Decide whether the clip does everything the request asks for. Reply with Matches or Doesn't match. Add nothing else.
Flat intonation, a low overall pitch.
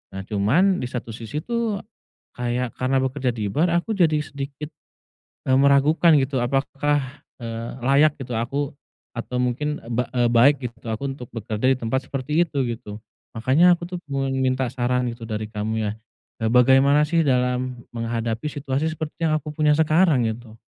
Doesn't match